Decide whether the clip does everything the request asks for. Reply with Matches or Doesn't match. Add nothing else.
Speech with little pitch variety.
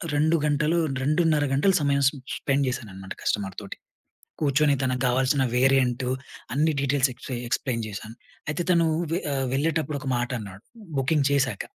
Doesn't match